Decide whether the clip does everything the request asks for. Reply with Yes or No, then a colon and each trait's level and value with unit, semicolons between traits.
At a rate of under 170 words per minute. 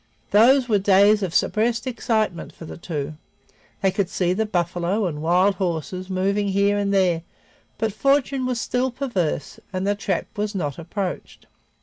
Yes: average, 160 wpm